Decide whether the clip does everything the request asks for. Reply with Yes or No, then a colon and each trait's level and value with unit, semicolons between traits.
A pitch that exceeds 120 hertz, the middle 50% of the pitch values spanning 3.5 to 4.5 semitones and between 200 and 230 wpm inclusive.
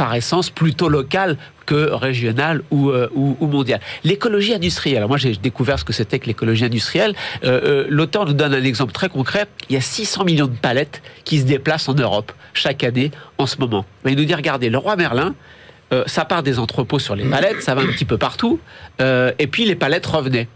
Yes: medium, 140 Hz; average, 3.8 semitones; fast, 220 wpm